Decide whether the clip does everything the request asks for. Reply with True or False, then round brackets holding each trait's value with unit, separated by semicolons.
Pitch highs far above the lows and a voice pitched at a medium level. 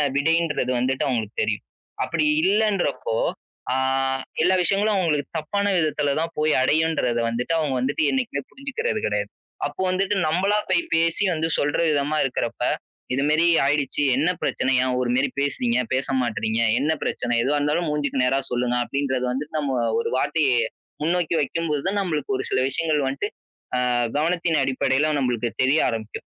False (4.2 semitones; 150 Hz)